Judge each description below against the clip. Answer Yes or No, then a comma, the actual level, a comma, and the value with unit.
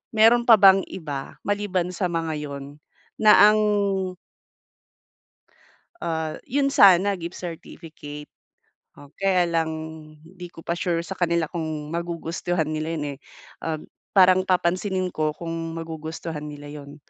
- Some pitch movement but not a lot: Yes, average, 3.0 semitones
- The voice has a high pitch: No, medium, 170 Hz